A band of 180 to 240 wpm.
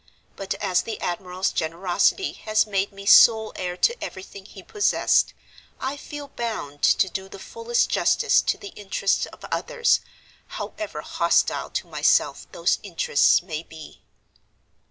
No: average, 140 wpm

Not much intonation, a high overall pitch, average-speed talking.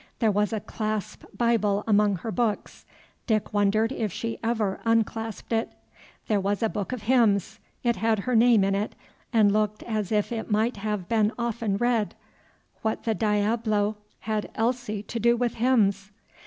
Yes: narrow, 1.9 semitones; high, 215 Hz; average, 170 wpm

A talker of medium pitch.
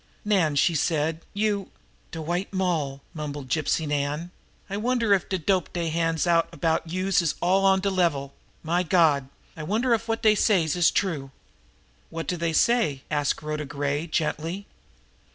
Yes: medium, 165 Hz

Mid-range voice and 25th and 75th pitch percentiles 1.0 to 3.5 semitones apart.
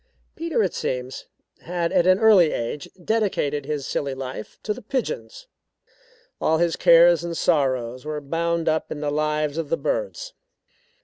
No: medium, 165 Hz; average, 4.3 semitones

